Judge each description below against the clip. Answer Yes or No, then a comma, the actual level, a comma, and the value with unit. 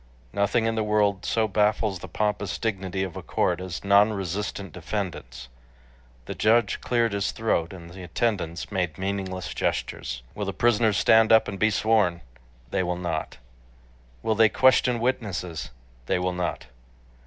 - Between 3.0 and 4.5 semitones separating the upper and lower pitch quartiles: Yes, average, 3.4 semitones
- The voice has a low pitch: Yes, low, 100 Hz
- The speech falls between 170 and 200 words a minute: No, average, 155 wpm